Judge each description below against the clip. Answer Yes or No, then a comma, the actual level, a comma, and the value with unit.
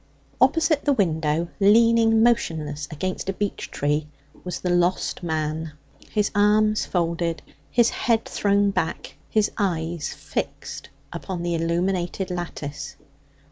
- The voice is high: No, medium, 180 Hz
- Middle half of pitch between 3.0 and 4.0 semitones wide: No, average, 4.4 semitones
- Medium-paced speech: No, slow, 120 wpm